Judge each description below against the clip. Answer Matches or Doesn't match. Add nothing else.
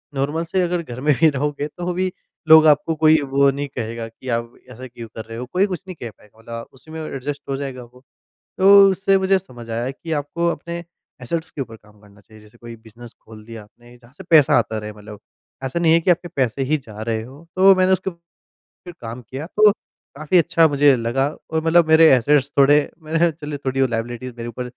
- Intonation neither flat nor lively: Doesn't match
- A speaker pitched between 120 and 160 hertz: Matches